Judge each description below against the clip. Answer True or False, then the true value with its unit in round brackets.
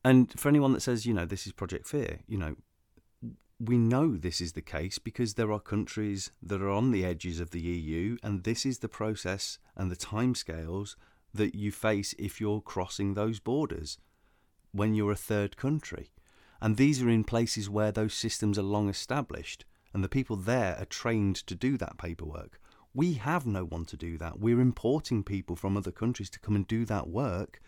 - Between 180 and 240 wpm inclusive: True (200 wpm)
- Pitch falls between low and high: False (105 Hz)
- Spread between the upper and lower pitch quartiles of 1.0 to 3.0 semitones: False (4.0 semitones)